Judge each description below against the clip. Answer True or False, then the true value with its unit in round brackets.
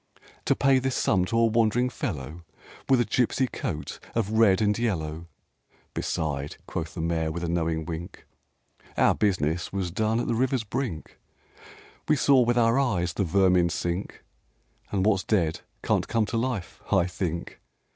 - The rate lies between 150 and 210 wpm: True (165 wpm)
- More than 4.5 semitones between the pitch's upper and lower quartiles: True (5.4 semitones)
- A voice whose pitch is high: False (100 Hz)